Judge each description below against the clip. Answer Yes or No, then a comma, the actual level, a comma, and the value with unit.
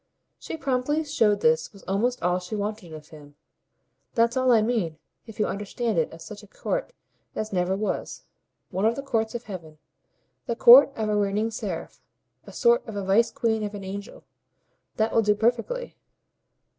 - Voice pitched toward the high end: Yes, high, 215 Hz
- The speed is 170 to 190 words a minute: Yes, average, 185 wpm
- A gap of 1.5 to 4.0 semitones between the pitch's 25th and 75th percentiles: Yes, average, 3.6 semitones